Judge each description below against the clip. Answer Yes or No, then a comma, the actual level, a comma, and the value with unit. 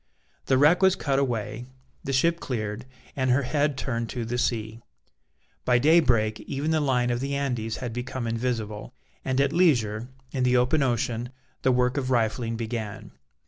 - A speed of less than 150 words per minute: No, average, 170 wpm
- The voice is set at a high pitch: No, low, 125 Hz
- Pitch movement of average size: Yes, average, 3.0 semitones